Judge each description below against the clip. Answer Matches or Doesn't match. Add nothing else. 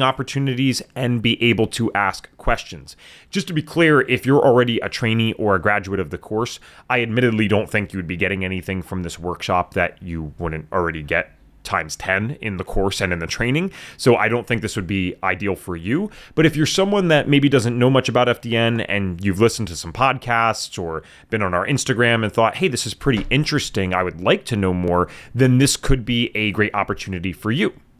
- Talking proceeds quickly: Matches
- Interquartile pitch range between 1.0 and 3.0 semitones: Doesn't match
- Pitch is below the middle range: Matches